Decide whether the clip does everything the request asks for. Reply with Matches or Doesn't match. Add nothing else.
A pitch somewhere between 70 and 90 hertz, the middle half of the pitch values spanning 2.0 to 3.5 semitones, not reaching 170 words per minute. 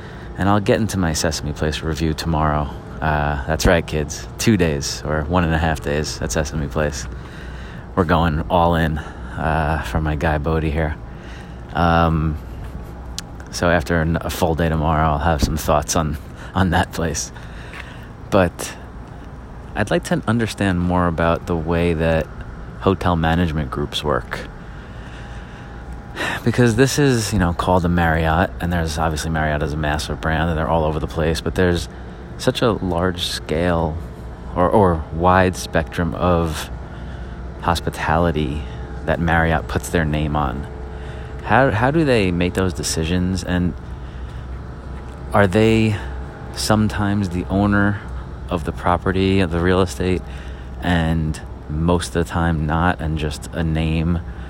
Matches